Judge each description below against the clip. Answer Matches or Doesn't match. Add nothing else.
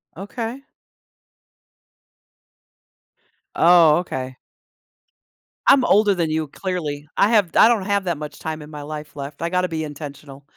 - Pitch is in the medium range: Matches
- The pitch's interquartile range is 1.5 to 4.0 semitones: Doesn't match